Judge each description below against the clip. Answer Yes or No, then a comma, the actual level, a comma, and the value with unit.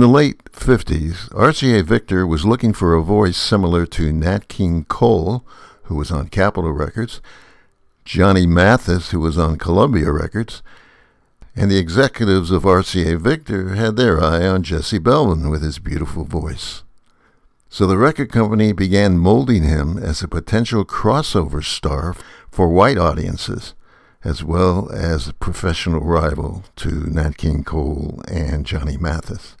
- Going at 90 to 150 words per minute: Yes, average, 145 wpm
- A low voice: Yes, very low, 90 Hz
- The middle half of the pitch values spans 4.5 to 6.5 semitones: Yes, average, 4.8 semitones